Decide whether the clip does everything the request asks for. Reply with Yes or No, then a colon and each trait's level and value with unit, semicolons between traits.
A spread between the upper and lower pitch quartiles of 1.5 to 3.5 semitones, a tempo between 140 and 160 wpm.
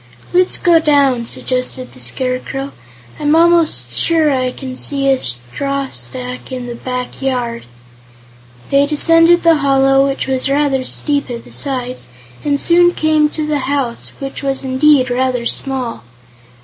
Yes: average, 2.7 semitones; average, 150 wpm